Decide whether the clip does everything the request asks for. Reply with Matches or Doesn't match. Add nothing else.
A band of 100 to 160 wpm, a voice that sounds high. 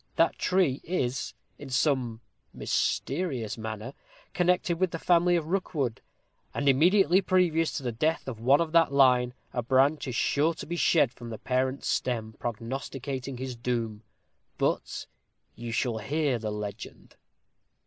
Doesn't match